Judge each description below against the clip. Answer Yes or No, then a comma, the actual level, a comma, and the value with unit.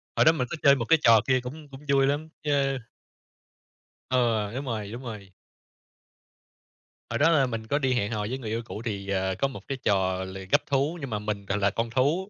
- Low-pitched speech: Yes, low, 120 Hz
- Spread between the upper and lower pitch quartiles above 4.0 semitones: Yes, average, 4.9 semitones